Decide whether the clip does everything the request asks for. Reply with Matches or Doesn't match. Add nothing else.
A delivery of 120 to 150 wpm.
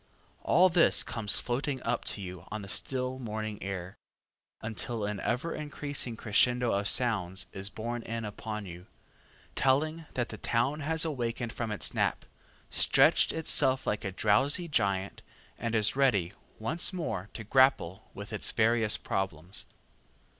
Matches